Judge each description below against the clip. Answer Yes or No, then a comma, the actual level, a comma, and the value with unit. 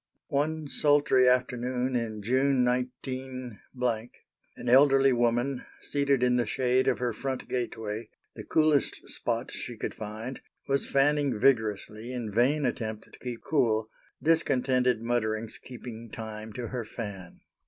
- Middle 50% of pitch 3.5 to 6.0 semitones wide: No, average, 2.9 semitones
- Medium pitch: No, low, 125 Hz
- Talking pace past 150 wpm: No, slow, 135 wpm